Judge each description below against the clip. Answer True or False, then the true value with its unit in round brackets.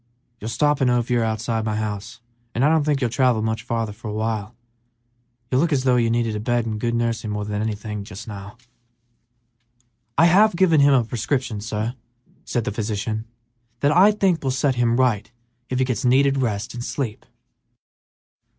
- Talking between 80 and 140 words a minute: False (195 wpm)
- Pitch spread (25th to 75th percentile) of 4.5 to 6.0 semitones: False (3.5 semitones)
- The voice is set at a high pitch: False (115 Hz)